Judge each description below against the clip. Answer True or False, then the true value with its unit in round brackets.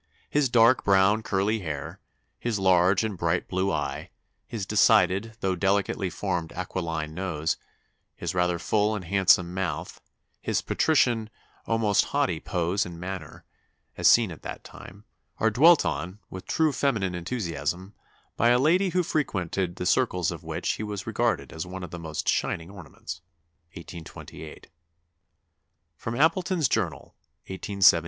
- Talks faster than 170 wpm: False (145 wpm)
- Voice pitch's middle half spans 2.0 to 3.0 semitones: False (4.1 semitones)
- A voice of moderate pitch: False (95 Hz)